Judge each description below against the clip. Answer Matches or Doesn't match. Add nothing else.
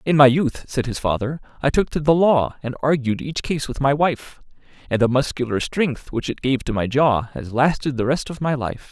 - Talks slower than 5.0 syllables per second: Doesn't match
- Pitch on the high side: Doesn't match